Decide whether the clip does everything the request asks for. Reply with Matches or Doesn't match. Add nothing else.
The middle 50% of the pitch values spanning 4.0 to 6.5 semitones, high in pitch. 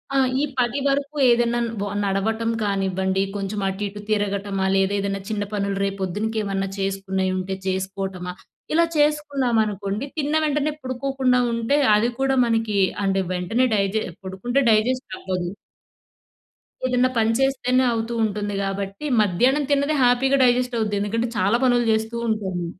Matches